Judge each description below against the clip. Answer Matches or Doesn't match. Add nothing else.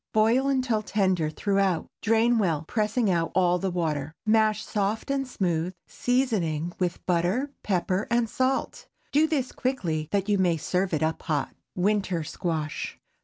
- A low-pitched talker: Doesn't match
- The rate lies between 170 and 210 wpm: Doesn't match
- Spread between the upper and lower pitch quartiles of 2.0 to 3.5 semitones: Doesn't match